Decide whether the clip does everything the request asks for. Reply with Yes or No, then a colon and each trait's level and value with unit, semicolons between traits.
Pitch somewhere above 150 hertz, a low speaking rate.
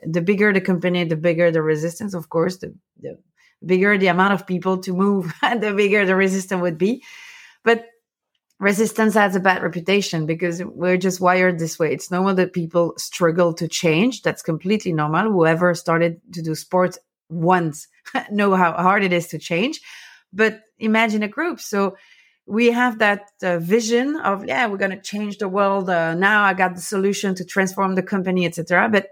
No: high, 190 Hz; average, 190 wpm